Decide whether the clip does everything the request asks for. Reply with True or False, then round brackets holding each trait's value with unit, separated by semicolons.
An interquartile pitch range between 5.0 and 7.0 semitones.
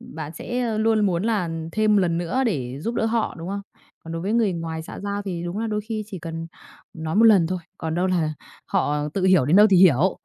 False (4.6 semitones)